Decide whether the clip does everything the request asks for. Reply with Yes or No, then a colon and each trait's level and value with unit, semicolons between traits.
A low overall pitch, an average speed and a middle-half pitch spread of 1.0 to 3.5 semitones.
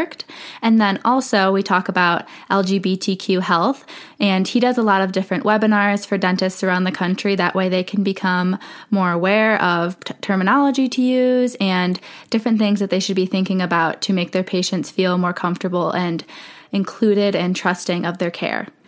No: high, 190 Hz; average, 180 wpm; average, 2.7 semitones